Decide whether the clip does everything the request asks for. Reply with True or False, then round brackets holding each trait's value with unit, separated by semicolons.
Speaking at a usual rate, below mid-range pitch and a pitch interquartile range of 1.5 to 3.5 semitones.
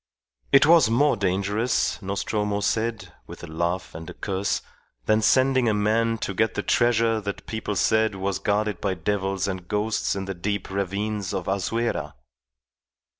True (160 wpm; 105 Hz; 2.5 semitones)